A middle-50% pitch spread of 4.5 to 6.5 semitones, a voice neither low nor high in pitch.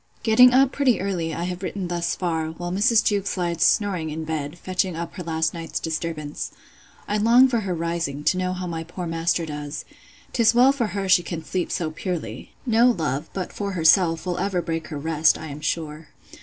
No: average, 3.6 semitones; medium, 175 Hz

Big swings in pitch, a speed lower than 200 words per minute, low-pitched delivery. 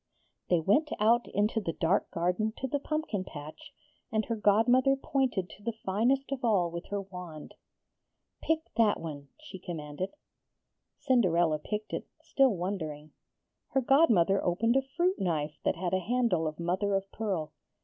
No: wide, 6.0 semitones; average, 160 wpm; high, 200 Hz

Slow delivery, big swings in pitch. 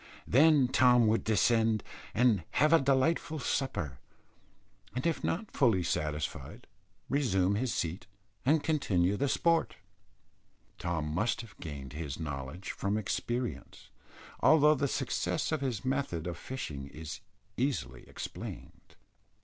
Yes: slow, 125 wpm; wide, 8.0 semitones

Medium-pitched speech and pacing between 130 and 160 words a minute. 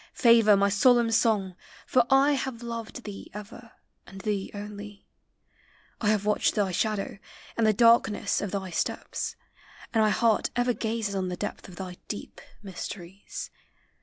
No: high, 210 Hz; average, 155 wpm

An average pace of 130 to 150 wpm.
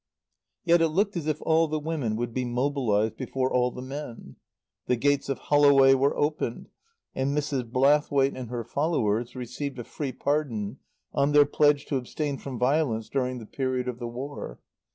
No: average, 175 wpm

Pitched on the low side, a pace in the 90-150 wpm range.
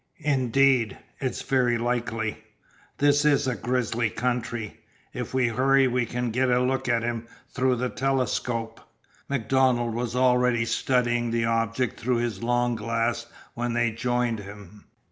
Yes: low, 120 Hz; average, 145 wpm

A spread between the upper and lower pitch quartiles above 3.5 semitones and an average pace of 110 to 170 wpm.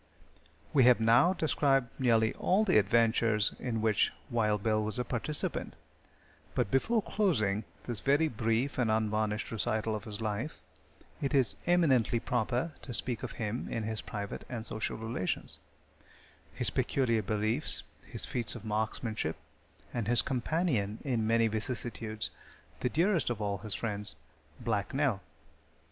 No: average, 3.1 semitones; average, 145 wpm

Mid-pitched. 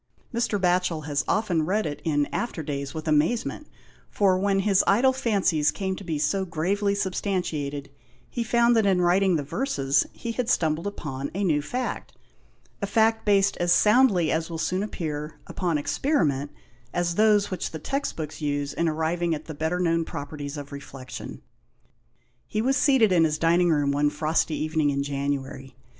Yes: medium, 170 Hz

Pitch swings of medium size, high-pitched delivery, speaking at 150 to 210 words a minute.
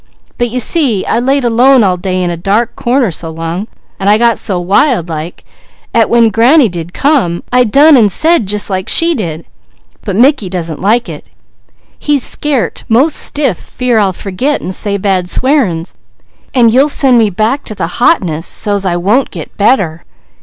No: wide, 5.7 semitones; high, 215 Hz; average, 180 wpm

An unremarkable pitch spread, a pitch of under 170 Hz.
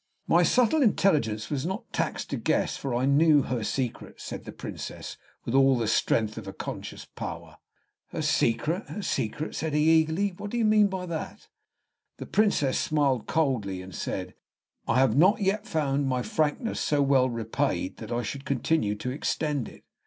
No: wide, 5.7 semitones; medium, 140 Hz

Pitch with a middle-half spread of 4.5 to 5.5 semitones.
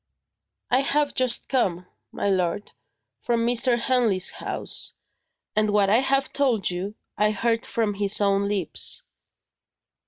No: average, 3.9 semitones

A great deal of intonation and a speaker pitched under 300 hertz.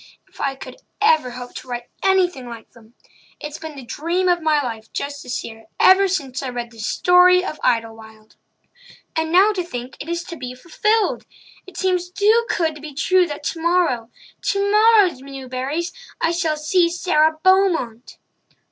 No: wide, 6.3 semitones; very high, 315 Hz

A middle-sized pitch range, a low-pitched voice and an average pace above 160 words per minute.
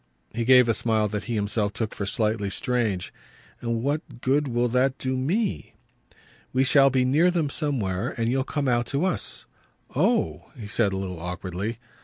Yes: average, 4.3 semitones; low, 120 Hz; average, 180 wpm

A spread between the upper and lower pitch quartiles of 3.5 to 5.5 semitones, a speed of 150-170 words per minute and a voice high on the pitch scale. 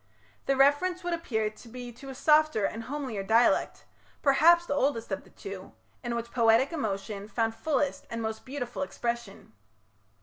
Yes: average, 4.4 semitones; average, 165 wpm; high, 240 Hz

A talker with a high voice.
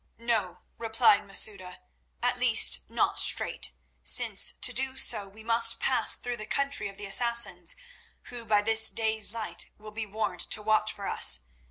Yes: high, 220 Hz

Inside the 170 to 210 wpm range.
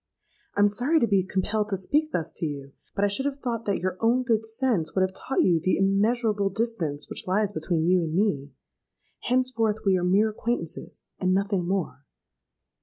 Yes: average, 195 wpm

